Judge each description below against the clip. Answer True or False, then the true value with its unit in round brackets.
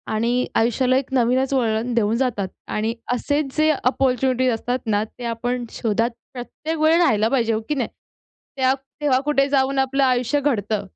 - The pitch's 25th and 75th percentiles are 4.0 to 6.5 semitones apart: False (2.9 semitones)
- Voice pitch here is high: True (250 Hz)